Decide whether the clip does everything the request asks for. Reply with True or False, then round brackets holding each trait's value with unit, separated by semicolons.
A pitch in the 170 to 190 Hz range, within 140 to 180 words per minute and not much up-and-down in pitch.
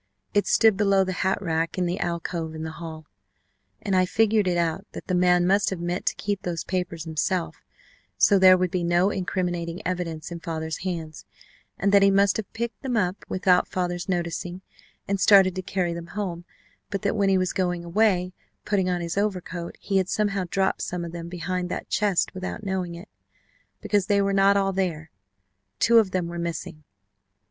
False (185 Hz; 195 wpm; 2.3 semitones)